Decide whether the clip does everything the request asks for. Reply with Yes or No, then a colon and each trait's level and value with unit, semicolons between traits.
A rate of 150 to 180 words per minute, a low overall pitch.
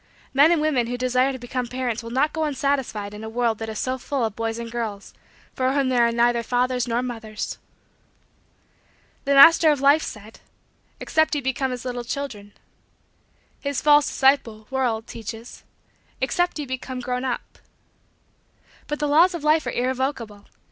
No: average, 170 wpm; very high, 255 Hz